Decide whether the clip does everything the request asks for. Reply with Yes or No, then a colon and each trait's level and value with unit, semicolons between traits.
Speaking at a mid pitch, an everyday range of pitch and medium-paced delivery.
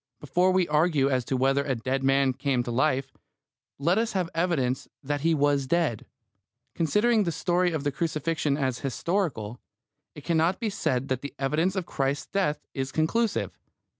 Yes: medium, 150 Hz; average, 4.4 semitones; average, 170 wpm